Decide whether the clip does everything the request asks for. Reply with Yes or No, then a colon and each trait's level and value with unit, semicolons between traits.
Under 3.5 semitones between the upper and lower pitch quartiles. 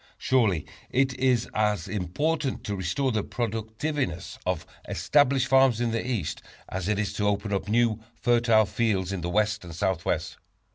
No: average, 4.3 semitones